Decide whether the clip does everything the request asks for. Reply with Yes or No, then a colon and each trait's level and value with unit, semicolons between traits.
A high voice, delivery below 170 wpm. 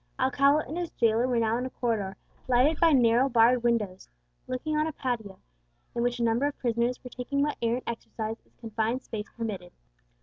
No: high, 240 Hz; average, 200 wpm